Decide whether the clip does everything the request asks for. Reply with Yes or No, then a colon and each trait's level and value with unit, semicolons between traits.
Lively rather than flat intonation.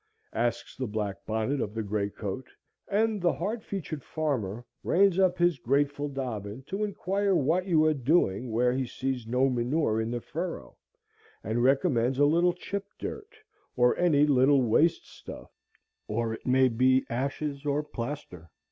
Yes: wide, 5.9 semitones